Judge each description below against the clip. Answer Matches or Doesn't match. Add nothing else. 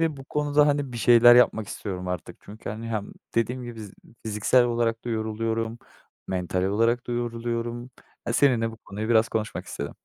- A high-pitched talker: Doesn't match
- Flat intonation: Matches